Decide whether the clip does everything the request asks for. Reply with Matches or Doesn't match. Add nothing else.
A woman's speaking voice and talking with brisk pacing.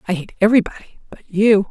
Doesn't match